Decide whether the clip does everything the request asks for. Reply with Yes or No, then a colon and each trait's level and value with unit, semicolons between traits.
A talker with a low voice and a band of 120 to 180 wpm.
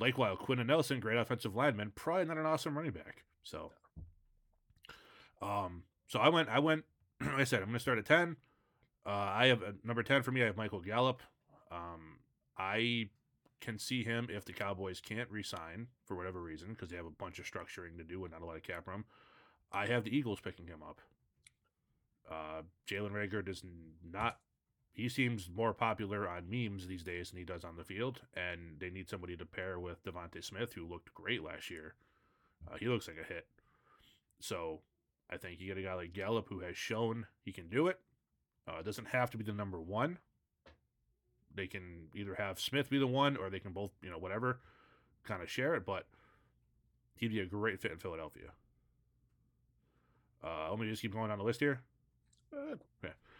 No: low, 105 Hz; average, 200 wpm